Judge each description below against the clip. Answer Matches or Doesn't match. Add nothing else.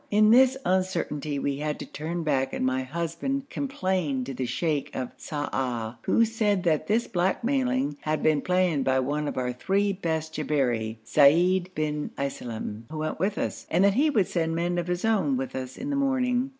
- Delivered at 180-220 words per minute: Matches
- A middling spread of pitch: Doesn't match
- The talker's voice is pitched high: Doesn't match